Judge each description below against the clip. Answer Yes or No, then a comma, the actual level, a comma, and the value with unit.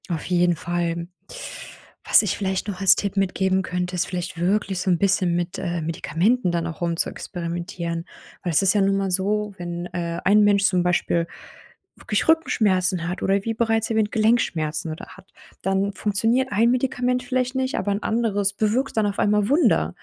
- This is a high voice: Yes, high, 195 Hz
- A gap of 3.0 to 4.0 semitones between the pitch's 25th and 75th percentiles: Yes, average, 3.5 semitones